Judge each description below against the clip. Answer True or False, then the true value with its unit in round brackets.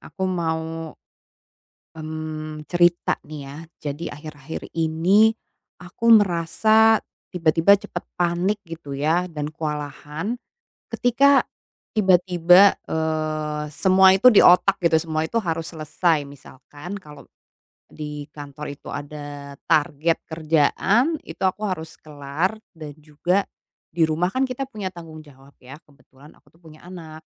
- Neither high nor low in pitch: True (160 Hz)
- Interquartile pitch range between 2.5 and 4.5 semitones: True (3.4 semitones)